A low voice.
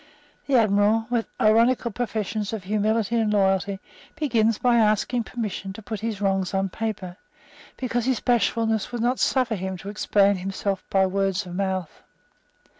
No: high, 210 Hz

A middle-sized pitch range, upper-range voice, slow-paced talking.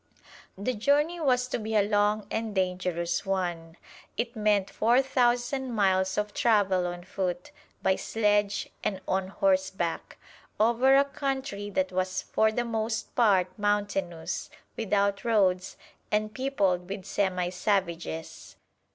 Yes: average, 3.7 semitones; high, 205 Hz; slow, 130 wpm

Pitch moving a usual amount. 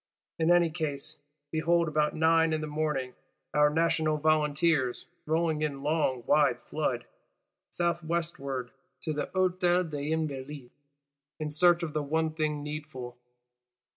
No: narrow, 1.8 semitones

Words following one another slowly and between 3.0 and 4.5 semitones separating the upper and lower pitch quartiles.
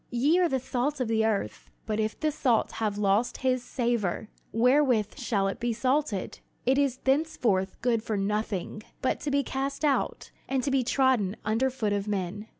No: average, 185 wpm; average, 4.1 semitones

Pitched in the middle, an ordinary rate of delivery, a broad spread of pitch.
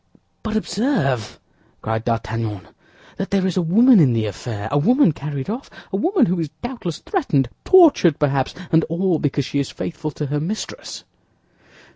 Yes: medium, 160 Hz; average, 160 wpm; wide, 8.0 semitones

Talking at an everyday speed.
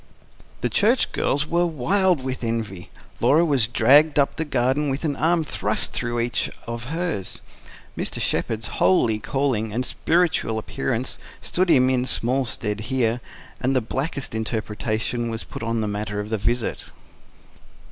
Yes: average, 155 wpm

